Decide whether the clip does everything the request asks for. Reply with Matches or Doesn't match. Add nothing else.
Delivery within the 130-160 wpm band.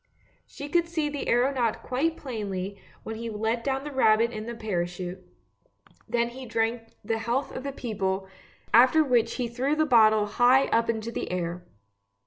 Doesn't match